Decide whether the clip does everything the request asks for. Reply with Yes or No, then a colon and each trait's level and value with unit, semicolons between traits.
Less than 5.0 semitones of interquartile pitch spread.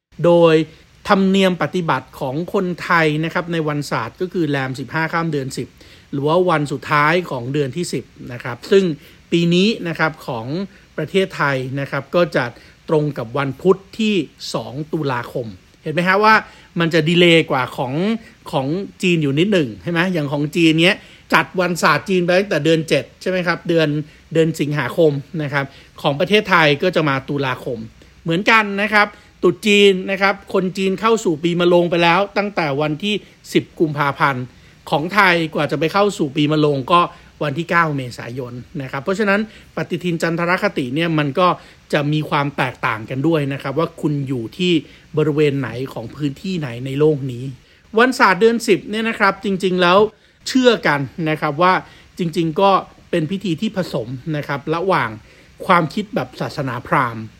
Yes: average, 4.1 semitones